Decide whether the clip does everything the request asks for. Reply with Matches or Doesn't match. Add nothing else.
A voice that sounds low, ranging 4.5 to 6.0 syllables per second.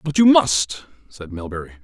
Matches